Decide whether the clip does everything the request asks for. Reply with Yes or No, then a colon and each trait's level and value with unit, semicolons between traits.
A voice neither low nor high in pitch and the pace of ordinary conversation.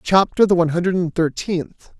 Yes: medium, 175 Hz; average, 180 wpm